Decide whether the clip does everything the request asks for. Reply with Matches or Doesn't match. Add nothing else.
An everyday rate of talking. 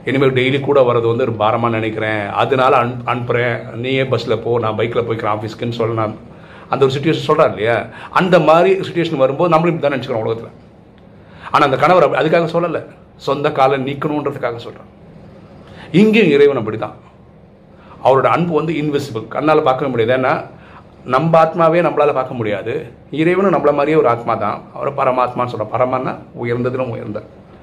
Doesn't match